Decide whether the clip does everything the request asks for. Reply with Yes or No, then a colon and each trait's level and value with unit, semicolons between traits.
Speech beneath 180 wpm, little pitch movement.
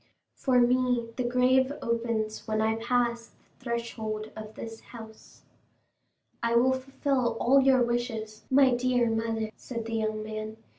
Yes: average, 145 wpm; narrow, 2.3 semitones